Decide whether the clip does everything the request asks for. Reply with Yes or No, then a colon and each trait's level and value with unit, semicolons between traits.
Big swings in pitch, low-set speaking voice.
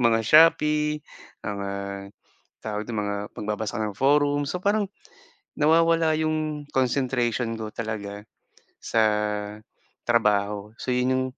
Yes: wide, 6.1 semitones; low, 115 Hz